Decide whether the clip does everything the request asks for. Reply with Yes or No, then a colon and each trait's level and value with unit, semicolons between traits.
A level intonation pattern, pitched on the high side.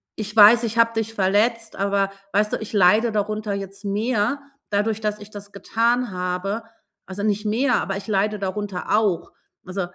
Yes: narrow, 2.0 semitones; high, 210 Hz